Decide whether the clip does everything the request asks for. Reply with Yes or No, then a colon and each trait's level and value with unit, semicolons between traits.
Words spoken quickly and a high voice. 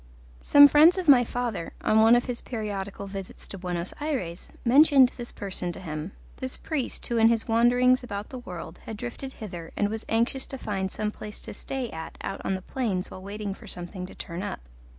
Yes: fast, 210 wpm; high, 215 Hz